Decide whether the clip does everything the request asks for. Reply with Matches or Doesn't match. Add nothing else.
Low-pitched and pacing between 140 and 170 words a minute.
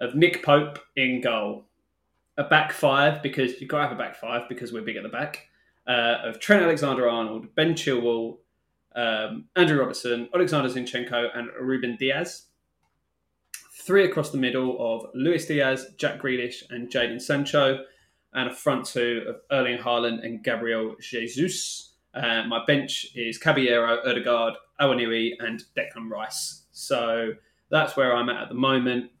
Matches